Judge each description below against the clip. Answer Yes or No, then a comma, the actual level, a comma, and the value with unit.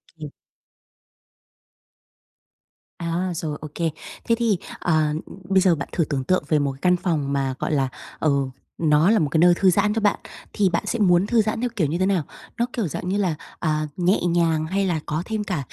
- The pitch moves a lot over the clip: No, average, 4.2 semitones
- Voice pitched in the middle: Yes, medium, 175 Hz